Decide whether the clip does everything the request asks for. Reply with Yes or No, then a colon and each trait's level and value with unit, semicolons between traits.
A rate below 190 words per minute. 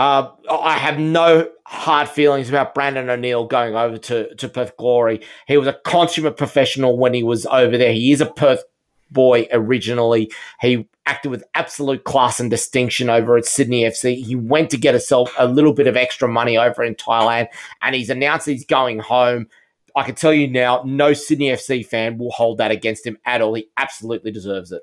No: average, 200 wpm